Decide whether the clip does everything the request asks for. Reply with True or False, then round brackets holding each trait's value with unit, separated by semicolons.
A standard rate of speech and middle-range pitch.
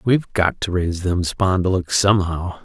False (160 wpm; 95 Hz)